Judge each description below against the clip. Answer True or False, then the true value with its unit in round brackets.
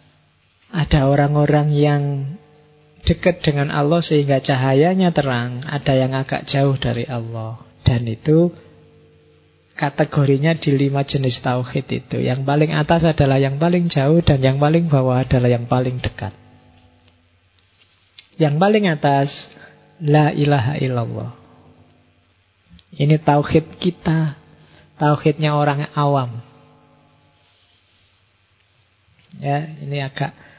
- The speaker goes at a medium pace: True (105 wpm)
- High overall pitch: False (140 Hz)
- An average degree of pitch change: True (4.9 semitones)